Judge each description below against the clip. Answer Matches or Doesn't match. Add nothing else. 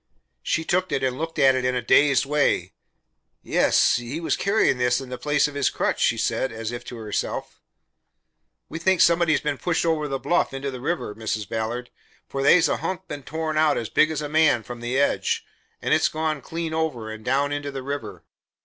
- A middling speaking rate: Doesn't match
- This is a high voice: Doesn't match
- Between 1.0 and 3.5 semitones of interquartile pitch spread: Doesn't match